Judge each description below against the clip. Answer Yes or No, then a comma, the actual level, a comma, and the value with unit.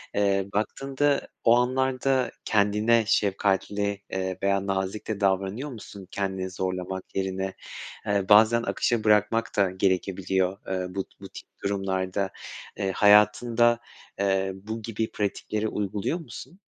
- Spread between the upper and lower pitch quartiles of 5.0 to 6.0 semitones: No, average, 2.8 semitones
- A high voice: No, low, 100 Hz